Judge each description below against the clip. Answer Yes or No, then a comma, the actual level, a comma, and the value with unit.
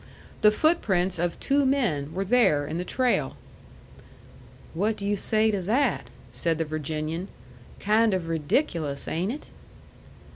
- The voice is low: No, medium, 185 Hz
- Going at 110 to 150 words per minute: Yes, average, 140 wpm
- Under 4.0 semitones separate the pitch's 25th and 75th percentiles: No, wide, 5.5 semitones